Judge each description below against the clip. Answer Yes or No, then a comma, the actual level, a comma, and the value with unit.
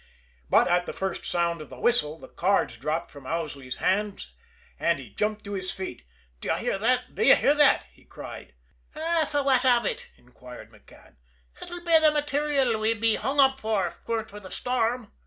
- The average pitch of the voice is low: No, high, 215 Hz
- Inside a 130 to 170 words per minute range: No, average, 195 wpm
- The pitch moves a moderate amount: No, wide, 7.6 semitones